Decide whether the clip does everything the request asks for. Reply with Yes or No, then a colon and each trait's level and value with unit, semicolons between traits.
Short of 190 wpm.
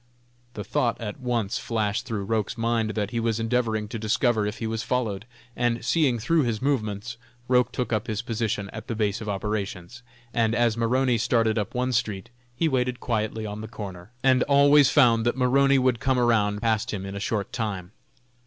No: average, 195 wpm